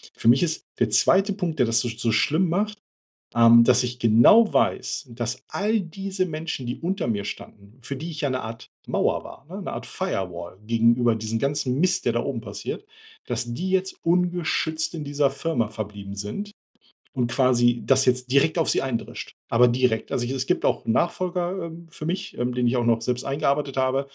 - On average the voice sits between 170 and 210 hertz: No, low, 135 Hz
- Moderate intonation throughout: No, wide, 6.3 semitones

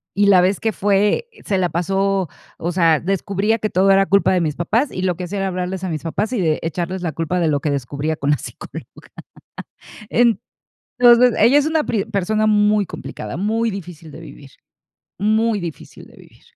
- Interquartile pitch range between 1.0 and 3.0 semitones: No, average, 4.0 semitones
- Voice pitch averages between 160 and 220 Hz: Yes, high, 190 Hz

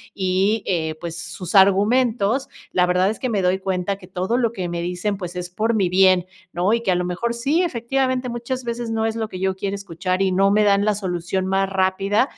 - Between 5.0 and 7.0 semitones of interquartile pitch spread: No, average, 3.7 semitones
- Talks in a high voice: Yes, high, 195 Hz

